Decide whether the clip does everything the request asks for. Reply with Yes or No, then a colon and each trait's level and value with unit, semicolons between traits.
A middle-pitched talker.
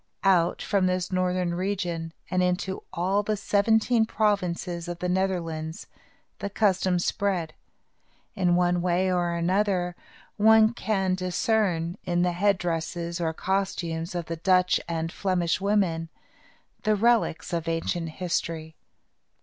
Yes: medium, 180 Hz